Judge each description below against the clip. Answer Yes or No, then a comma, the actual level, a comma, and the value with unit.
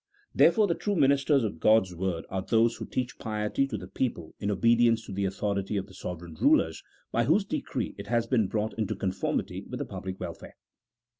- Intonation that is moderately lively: Yes, average, 4.1 semitones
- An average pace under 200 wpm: No, fast, 205 wpm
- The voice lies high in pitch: No, low, 110 Hz